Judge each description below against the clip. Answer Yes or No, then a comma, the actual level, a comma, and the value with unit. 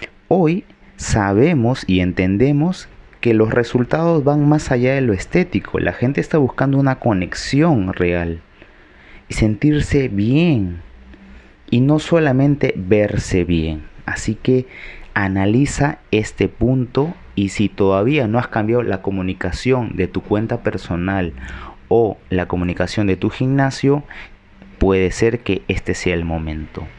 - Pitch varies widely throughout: Yes, wide, 5.9 semitones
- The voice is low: Yes, low, 105 Hz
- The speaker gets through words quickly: No, average, 130 wpm